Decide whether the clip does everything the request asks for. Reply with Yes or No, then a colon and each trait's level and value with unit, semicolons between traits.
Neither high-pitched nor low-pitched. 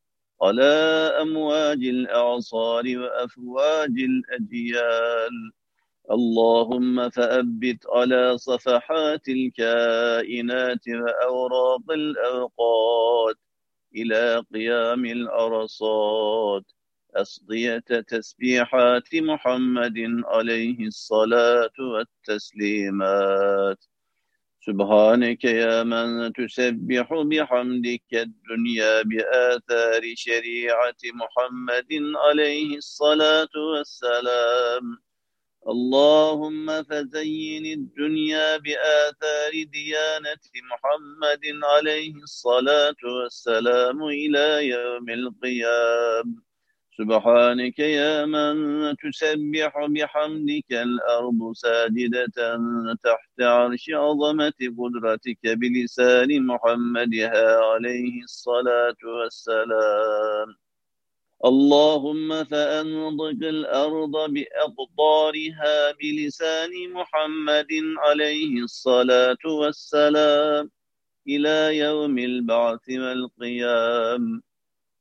No: low, 125 Hz